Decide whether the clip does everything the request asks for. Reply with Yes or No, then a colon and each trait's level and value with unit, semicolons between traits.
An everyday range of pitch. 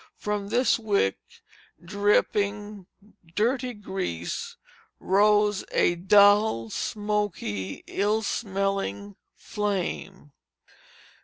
No: narrow, 2.2 semitones